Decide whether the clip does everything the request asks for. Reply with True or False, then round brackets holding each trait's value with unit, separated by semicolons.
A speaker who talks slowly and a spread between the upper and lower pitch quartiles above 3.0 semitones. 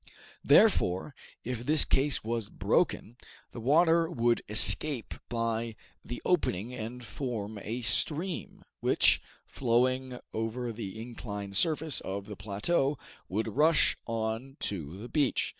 True (125 wpm; 4.0 semitones)